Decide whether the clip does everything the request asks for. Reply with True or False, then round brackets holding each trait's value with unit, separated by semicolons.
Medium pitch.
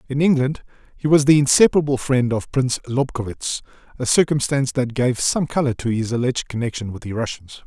False (130 Hz)